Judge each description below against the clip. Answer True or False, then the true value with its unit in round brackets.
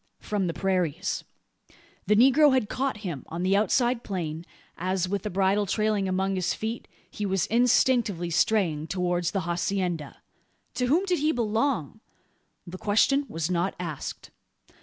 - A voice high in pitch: True (195 Hz)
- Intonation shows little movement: False (4.5 semitones)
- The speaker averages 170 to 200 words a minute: False (150 wpm)